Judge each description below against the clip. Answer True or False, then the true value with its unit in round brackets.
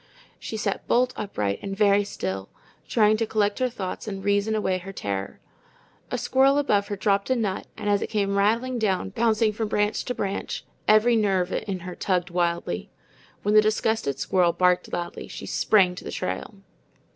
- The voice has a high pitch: True (205 Hz)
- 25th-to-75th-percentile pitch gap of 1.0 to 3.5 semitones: True (2.9 semitones)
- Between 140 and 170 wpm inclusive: False (180 wpm)